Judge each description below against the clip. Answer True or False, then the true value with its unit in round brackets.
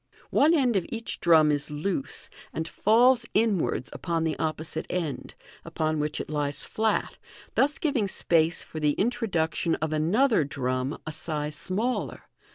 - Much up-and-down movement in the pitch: True (6.6 semitones)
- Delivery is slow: False (150 wpm)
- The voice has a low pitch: False (165 Hz)